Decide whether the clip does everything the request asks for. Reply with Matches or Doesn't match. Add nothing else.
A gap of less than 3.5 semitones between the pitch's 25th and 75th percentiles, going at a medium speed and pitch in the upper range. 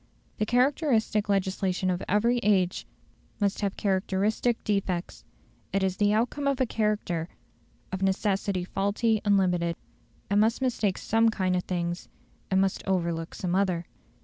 Matches